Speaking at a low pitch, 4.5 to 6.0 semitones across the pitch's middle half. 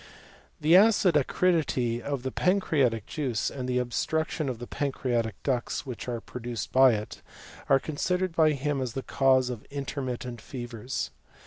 No: low, 130 Hz; average, 3.6 semitones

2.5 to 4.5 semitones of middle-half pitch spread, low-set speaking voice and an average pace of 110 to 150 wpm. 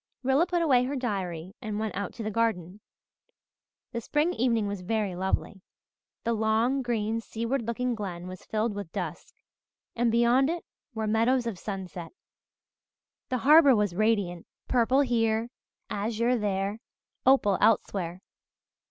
No: average, 3.5 semitones; high, 225 Hz; average, 140 wpm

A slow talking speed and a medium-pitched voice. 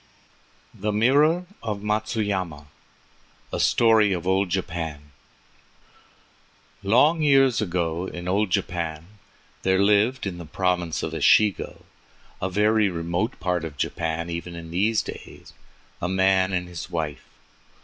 No: slow, 125 wpm; very low, 95 Hz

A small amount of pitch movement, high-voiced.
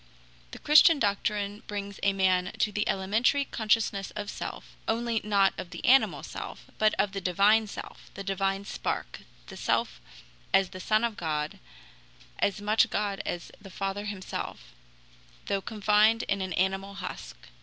Yes: narrow, 1.8 semitones; high, 200 Hz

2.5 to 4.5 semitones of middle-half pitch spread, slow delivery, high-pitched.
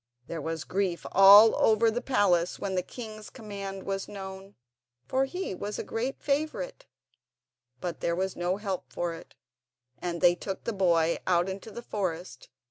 No: average, 3.4 semitones; average, 165 wpm; high, 195 Hz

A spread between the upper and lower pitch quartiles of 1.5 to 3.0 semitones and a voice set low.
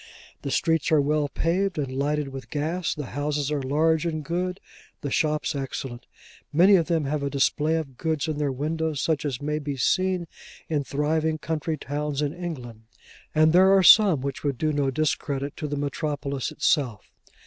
No: narrow, 2.4 semitones; medium, 150 Hz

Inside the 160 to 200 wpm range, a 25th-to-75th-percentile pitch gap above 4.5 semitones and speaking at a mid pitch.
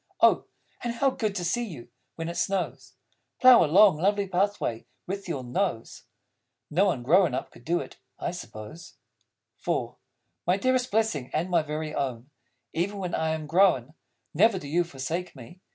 Yes: average, 170 wpm; average, 5.1 semitones; medium, 175 Hz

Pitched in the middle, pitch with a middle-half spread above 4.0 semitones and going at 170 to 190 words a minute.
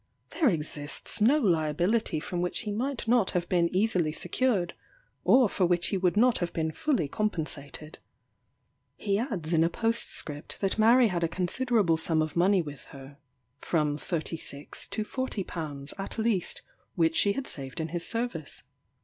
No: medium, 175 Hz; wide, 5.6 semitones; average, 160 wpm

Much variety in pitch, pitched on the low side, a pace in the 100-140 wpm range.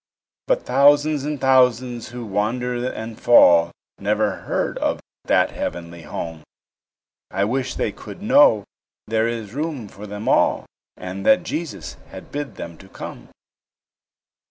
Yes: wide, 5.7 semitones; low, 120 Hz; slow, 135 wpm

